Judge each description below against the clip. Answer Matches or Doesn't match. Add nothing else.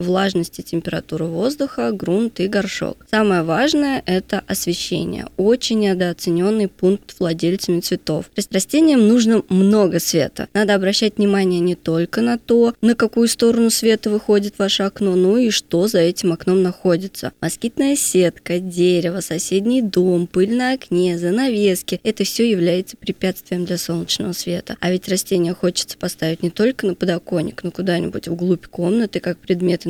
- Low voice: Doesn't match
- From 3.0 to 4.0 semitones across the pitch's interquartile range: Matches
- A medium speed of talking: Matches